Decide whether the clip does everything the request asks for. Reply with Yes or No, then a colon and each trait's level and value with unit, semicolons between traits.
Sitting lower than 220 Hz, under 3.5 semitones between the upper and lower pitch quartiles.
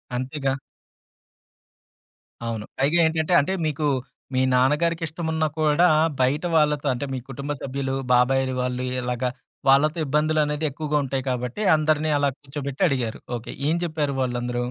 Yes: medium, 140 Hz; average, 3.1 semitones